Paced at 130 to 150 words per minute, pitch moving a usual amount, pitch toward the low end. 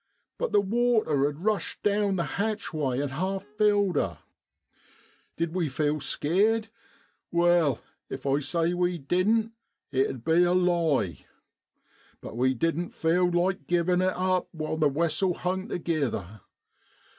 No: average, 140 wpm; average, 4.4 semitones; medium, 175 Hz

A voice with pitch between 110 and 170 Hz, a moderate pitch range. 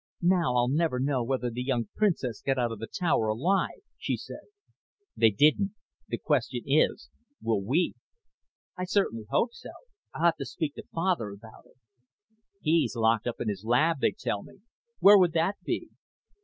No: low, 135 Hz; wide, 7.0 semitones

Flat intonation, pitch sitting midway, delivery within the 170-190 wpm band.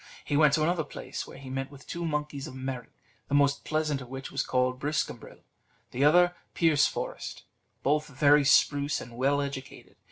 Yes: narrow, 2.1 semitones; medium, 145 Hz; average, 180 wpm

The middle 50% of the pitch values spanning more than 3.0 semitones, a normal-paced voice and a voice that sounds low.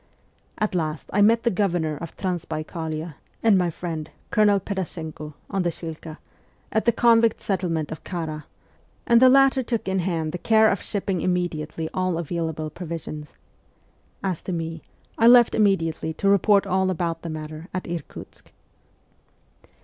No: average, 3.9 semitones; average, 150 wpm; medium, 175 Hz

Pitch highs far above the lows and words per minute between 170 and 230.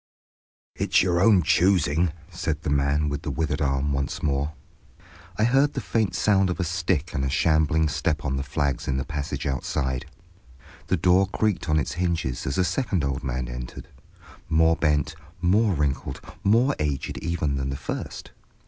No: average, 4.4 semitones; average, 175 wpm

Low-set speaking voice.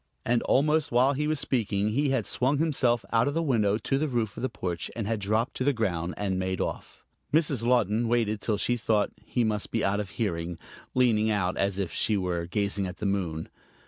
Yes: low, 110 Hz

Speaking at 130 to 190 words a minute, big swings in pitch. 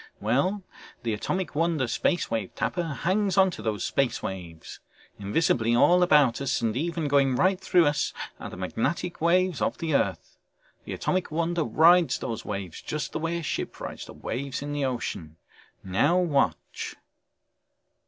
Yes: average, 160 wpm; wide, 6.9 semitones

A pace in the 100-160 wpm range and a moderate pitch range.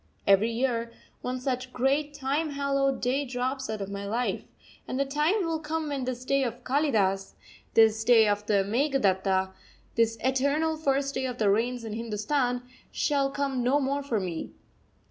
No: average, 170 wpm; average, 3.9 semitones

